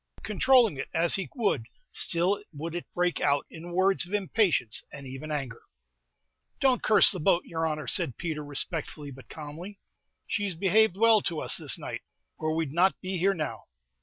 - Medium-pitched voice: Yes, medium, 170 Hz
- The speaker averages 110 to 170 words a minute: No, average, 180 wpm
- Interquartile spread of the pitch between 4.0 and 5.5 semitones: Yes, average, 4.5 semitones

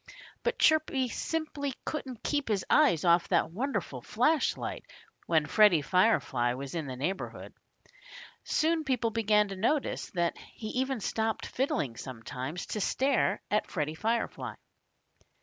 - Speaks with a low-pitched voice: No, high, 210 Hz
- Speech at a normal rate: No, slow, 130 wpm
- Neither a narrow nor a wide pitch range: No, wide, 8.3 semitones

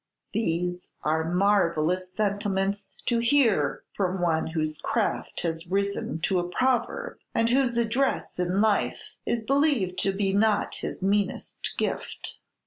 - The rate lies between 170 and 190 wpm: No, slow, 135 wpm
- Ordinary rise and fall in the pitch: Yes, average, 4.0 semitones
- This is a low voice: No, high, 195 Hz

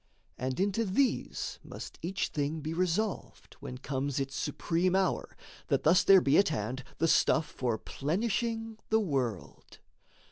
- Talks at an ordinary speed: Yes, average, 145 wpm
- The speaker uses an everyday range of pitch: No, wide, 6.2 semitones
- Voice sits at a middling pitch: Yes, medium, 165 Hz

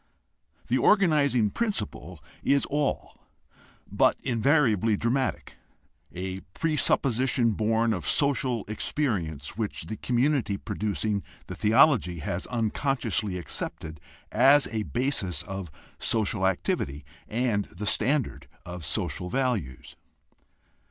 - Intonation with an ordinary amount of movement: No, wide, 5.7 semitones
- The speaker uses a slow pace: Yes, slow, 100 wpm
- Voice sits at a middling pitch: No, low, 110 Hz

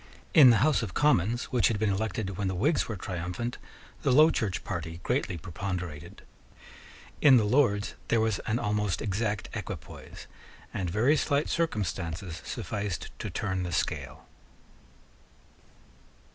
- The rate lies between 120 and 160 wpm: Yes, average, 140 wpm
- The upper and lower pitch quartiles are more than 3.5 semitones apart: Yes, average, 4.8 semitones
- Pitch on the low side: Yes, low, 105 Hz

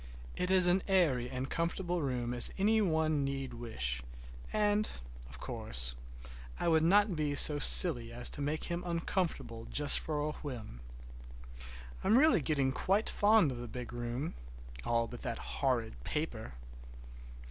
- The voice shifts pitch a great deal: Yes, wide, 6.6 semitones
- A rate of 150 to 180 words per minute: Yes, average, 155 wpm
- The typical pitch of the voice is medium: Yes, medium, 145 Hz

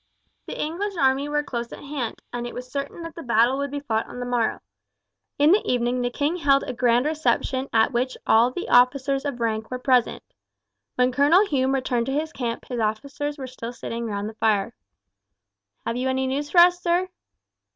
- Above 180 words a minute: Yes, fast, 205 wpm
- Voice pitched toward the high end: Yes, very high, 260 Hz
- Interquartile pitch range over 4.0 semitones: No, average, 3.3 semitones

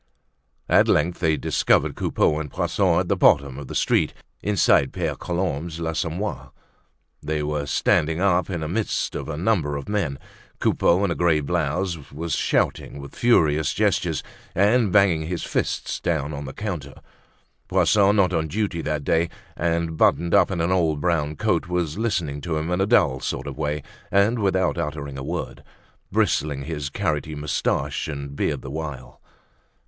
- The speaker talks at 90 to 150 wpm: No, average, 170 wpm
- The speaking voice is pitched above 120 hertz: No, very low, 80 Hz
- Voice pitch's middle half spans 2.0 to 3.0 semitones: No, average, 3.7 semitones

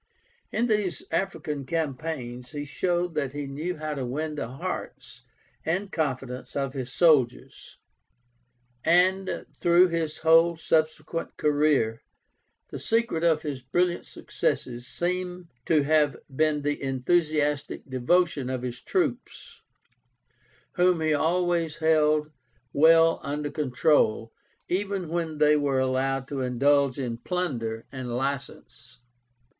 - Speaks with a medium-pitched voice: Yes, medium, 150 Hz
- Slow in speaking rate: Yes, slow, 120 wpm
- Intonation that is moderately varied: Yes, average, 3.9 semitones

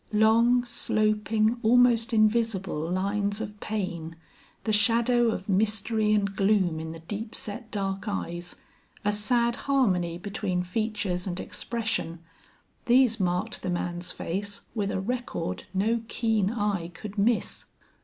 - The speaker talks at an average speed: No, slow, 130 wpm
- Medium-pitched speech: No, high, 210 Hz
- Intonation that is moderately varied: Yes, average, 3.2 semitones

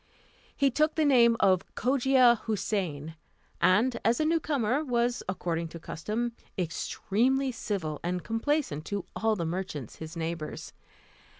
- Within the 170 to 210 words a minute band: No, slow, 135 wpm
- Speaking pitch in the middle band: No, high, 215 Hz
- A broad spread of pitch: Yes, wide, 7.0 semitones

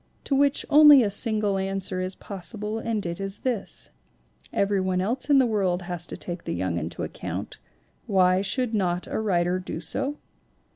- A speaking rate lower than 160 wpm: No, average, 175 wpm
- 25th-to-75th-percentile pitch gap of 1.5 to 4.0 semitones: Yes, average, 3.7 semitones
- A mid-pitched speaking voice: No, high, 195 Hz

